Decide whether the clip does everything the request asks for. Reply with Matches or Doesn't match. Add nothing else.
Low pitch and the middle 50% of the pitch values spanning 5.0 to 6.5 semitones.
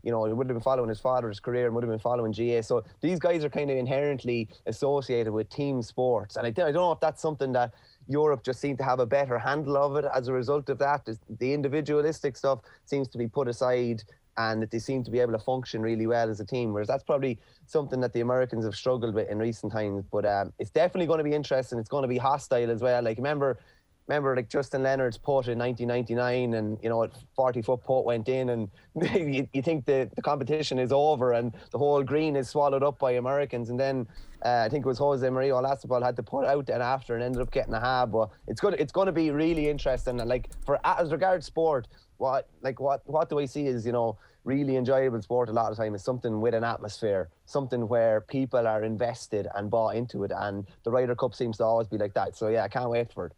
Doesn't match